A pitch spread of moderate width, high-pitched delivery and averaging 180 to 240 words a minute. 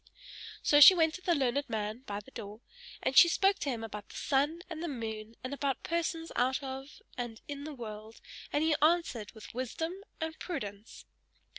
No: wide, 6.2 semitones; very high, 270 Hz; average, 190 wpm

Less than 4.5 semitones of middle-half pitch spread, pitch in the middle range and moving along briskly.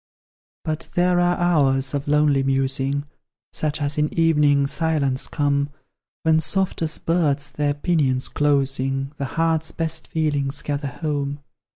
No: narrow, 2.5 semitones; medium, 145 Hz; slow, 135 wpm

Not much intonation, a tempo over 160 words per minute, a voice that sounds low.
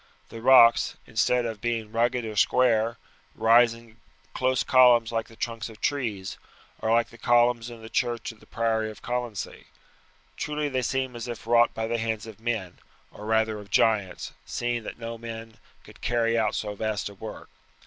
Yes: narrow, 1.3 semitones; average, 185 wpm; low, 115 Hz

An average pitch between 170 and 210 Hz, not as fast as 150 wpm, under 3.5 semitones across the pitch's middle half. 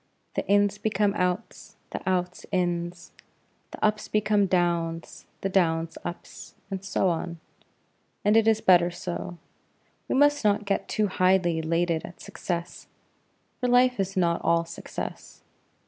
Yes: medium, 185 Hz; average, 140 wpm; average, 3.1 semitones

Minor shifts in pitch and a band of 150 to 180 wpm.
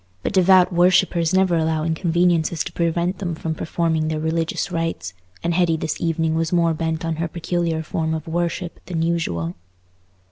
Yes: narrow, 1.4 semitones; average, 170 wpm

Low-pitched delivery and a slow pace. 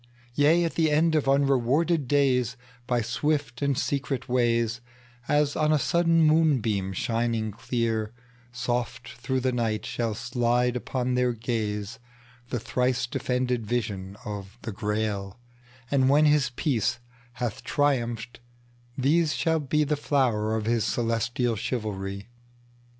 Yes: low, 125 Hz; slow, 115 wpm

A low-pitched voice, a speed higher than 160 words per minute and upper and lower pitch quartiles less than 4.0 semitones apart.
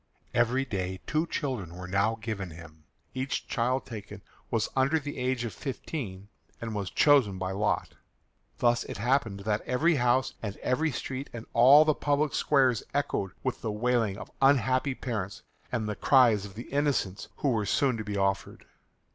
No: low, 120 Hz; average, 170 wpm; average, 4.8 semitones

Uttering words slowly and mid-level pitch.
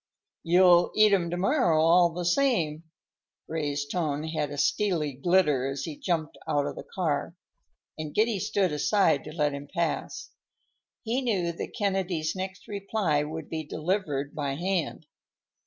No: average, 155 wpm; medium, 170 Hz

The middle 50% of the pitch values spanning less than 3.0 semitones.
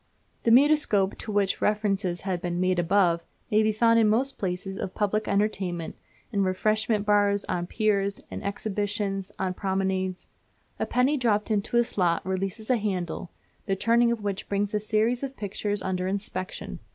Yes: narrow, 2.4 semitones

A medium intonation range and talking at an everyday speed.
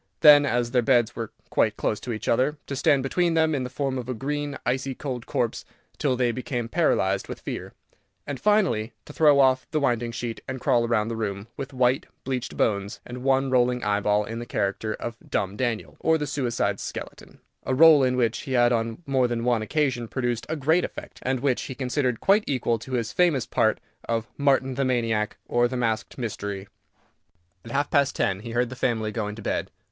No: average, 3.1 semitones; fast, 210 wpm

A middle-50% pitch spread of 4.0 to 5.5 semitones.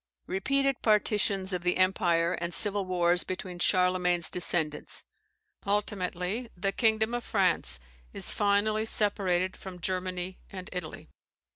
No: narrow, 2.5 semitones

